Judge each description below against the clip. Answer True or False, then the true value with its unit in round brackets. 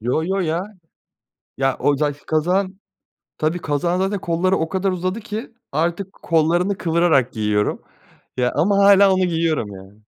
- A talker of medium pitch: True (170 Hz)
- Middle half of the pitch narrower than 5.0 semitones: True (4.5 semitones)